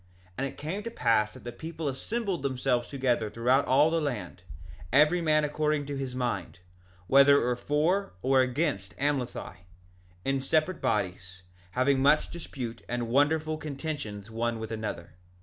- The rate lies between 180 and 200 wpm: No, average, 160 wpm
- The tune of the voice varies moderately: Yes, average, 4.4 semitones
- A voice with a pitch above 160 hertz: No, low, 135 Hz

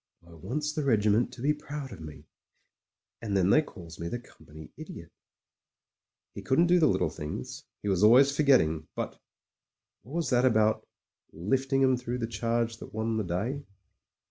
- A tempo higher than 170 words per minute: Yes, average, 180 wpm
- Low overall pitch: Yes, low, 115 Hz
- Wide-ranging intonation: Yes, wide, 5.7 semitones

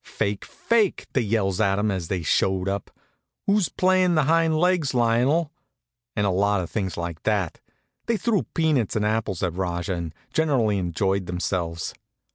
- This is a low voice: Yes, low, 105 Hz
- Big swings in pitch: Yes, wide, 9.0 semitones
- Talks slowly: No, average, 165 wpm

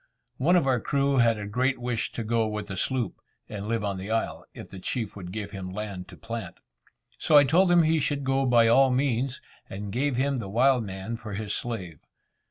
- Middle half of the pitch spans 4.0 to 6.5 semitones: Yes, average, 4.6 semitones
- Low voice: Yes, low, 115 Hz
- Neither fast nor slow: No, fast, 220 wpm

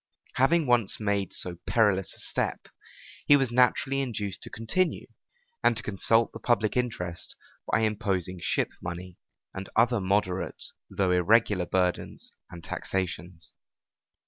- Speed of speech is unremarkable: No, slow, 130 wpm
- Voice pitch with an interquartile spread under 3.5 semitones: No, average, 4.4 semitones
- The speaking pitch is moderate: No, low, 100 Hz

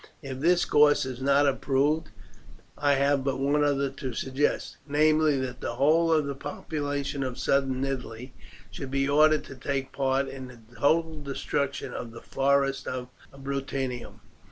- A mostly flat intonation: Yes, narrow, 1.6 semitones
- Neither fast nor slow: Yes, average, 155 wpm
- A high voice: No, medium, 140 Hz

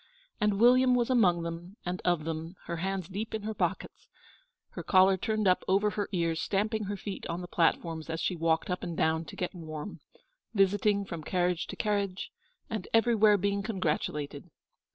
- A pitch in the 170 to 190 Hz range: Yes, medium, 185 Hz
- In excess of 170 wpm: Yes, average, 180 wpm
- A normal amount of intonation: Yes, average, 3.7 semitones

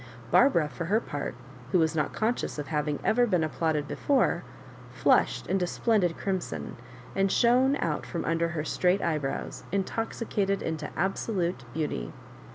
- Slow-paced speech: No, average, 145 wpm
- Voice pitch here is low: No, medium, 170 Hz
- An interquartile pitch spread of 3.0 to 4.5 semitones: No, average, 5.0 semitones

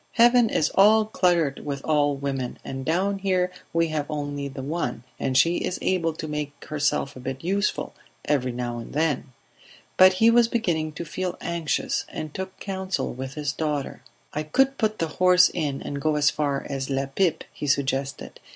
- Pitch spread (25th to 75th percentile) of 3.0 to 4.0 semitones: No, average, 4.7 semitones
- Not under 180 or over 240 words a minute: Yes, average, 190 wpm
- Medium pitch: Yes, medium, 155 Hz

